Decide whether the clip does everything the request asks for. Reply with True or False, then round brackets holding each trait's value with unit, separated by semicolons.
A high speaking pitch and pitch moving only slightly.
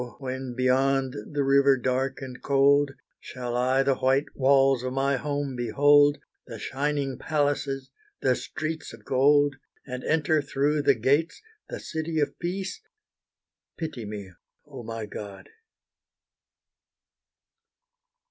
False (135 Hz; 2.2 semitones)